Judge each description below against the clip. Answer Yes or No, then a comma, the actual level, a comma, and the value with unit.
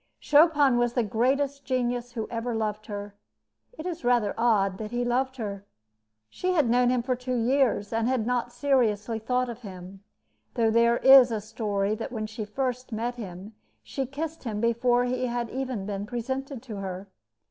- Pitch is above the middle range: Yes, high, 240 Hz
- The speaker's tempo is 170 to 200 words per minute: Yes, average, 180 wpm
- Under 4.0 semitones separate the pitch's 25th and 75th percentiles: Yes, average, 2.9 semitones